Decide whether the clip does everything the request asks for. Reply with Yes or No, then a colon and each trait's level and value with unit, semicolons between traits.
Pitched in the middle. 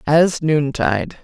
Yes: medium, 160 Hz